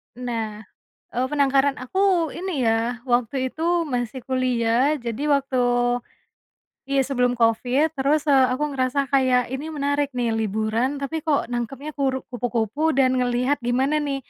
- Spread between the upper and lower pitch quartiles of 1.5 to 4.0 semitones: Yes, average, 2.7 semitones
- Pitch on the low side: No, very high, 260 Hz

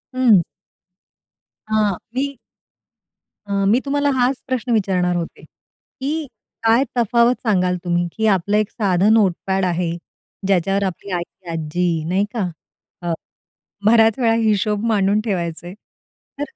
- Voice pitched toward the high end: Yes, high, 200 Hz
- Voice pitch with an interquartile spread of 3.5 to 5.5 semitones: Yes, average, 4.2 semitones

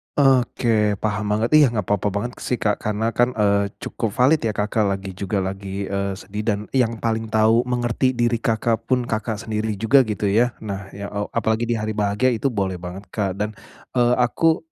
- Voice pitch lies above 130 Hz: No, low, 110 Hz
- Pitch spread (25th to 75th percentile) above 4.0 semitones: No, average, 2.8 semitones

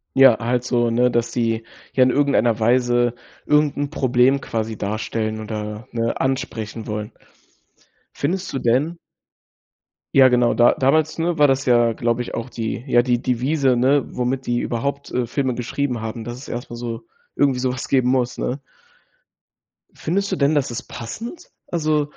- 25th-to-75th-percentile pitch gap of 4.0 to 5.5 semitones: No, average, 2.9 semitones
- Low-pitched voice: Yes, low, 125 Hz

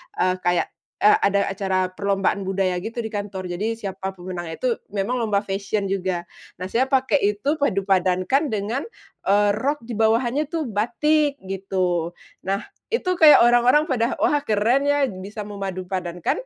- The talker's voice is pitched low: No, high, 205 Hz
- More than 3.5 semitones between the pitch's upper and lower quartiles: Yes, average, 4.5 semitones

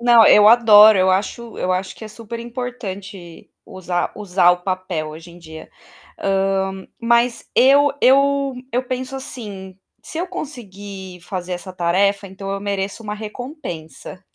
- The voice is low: No, high, 200 Hz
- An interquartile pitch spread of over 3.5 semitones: Yes, average, 4.3 semitones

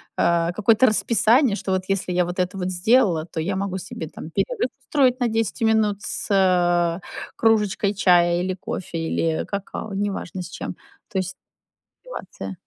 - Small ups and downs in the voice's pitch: No, average, 3.4 semitones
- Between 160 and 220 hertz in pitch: Yes, high, 190 Hz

